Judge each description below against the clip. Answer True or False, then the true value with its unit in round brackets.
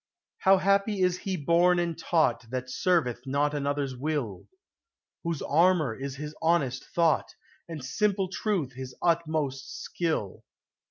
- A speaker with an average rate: False (130 wpm)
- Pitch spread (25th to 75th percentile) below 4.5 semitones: False (4.9 semitones)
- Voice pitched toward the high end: False (155 Hz)